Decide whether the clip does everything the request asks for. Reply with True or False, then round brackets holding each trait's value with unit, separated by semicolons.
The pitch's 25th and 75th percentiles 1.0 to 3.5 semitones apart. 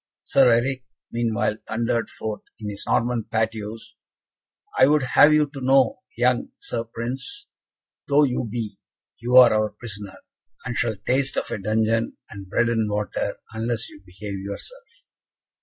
True (2.9 semitones)